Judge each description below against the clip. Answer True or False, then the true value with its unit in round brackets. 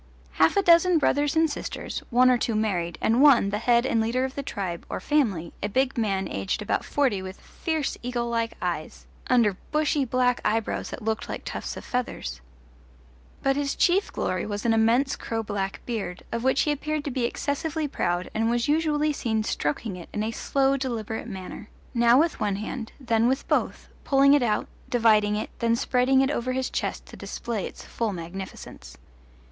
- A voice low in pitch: False (235 Hz)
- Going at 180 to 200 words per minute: True (190 wpm)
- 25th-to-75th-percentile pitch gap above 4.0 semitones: True (4.4 semitones)